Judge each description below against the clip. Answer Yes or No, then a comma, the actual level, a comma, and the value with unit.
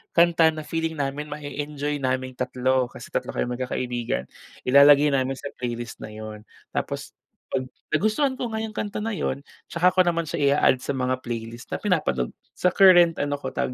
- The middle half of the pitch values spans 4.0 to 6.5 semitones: Yes, average, 4.7 semitones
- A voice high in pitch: No, medium, 140 Hz